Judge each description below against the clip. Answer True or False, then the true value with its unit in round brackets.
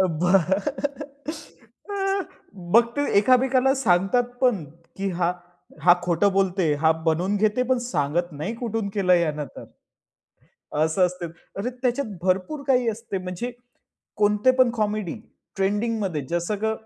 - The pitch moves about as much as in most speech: False (5.8 semitones)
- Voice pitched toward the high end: True (205 Hz)